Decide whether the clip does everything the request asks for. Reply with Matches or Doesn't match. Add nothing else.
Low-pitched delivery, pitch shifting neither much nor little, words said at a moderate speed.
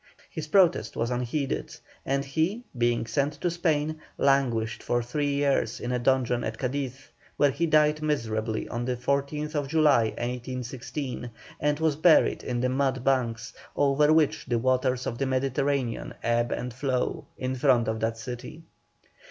Matches